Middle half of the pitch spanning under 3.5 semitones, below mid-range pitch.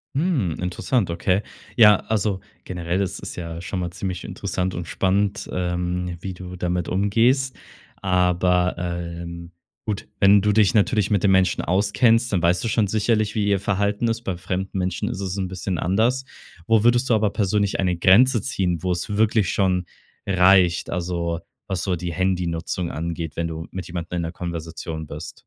Yes: average, 2.8 semitones; very low, 95 Hz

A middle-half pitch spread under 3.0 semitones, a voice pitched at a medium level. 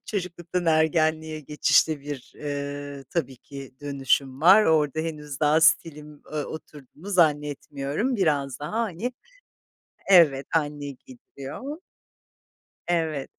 Yes: narrow, 2.6 semitones; medium, 150 Hz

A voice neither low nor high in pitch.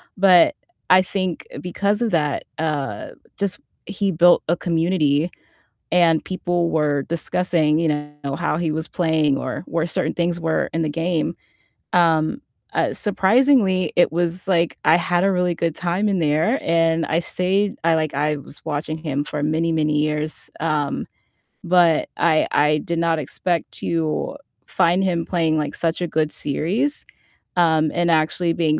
Yes: medium, 165 Hz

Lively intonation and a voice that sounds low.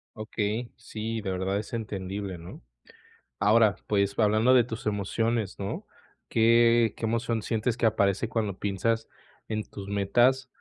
No: narrow, 2.5 semitones; low, 110 Hz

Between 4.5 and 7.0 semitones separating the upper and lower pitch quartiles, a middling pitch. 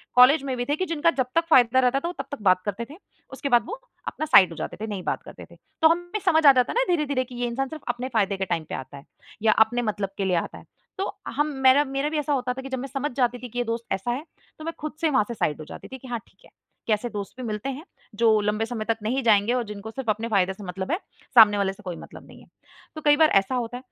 No: average, 4.8 semitones; high, 245 Hz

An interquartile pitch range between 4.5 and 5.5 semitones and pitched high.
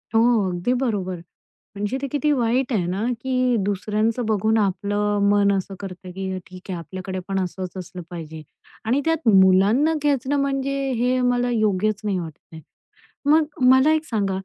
Yes: average, 5.0 semitones; high, 210 Hz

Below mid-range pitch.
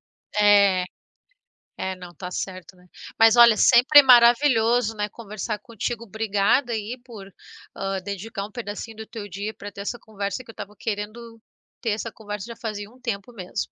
No: high, 215 Hz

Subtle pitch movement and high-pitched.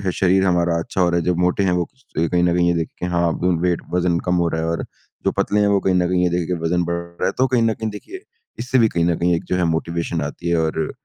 No: narrow, 1.5 semitones; very low, 90 Hz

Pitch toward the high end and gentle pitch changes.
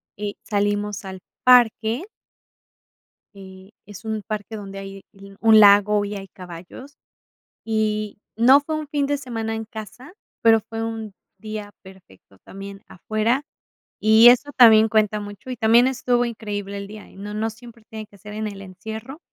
Yes: high, 215 Hz; narrow, 2.0 semitones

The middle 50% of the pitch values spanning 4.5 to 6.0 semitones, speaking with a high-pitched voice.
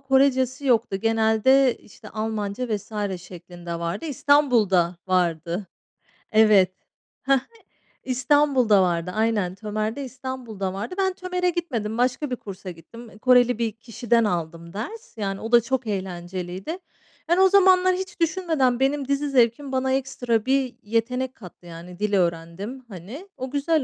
Yes: wide, 5.6 semitones; high, 230 Hz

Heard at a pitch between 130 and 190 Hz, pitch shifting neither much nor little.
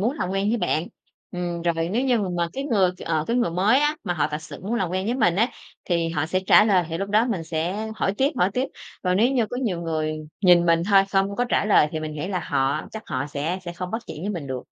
Yes: medium, 185 Hz; average, 4.6 semitones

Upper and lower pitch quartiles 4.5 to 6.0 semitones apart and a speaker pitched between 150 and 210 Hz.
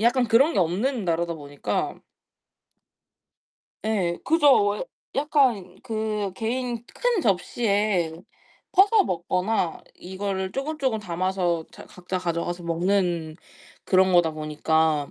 Yes: wide, 5.4 semitones; high, 190 Hz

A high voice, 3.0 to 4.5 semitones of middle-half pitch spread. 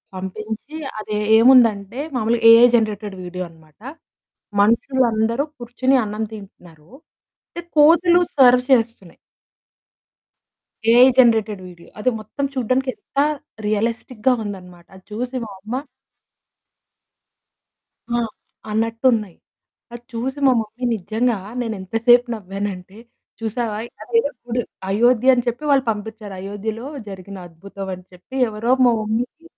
Yes: high, 225 Hz; average, 3.4 semitones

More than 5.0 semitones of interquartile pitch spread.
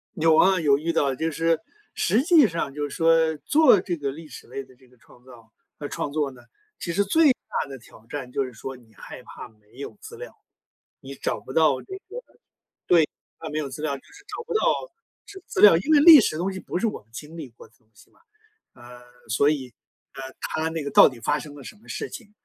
Yes: wide, 5.5 semitones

